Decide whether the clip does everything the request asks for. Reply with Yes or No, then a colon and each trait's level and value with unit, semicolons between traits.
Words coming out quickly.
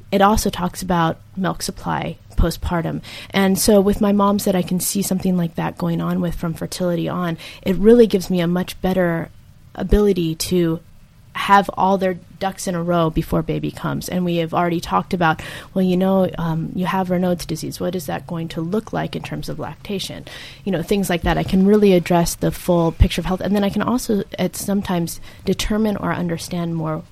Yes: fast, 210 wpm